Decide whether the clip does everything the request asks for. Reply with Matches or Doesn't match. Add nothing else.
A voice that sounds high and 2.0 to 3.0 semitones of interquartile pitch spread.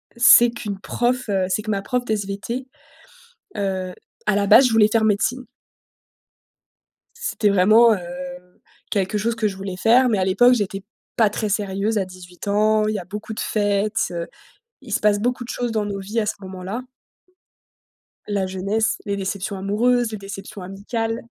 Matches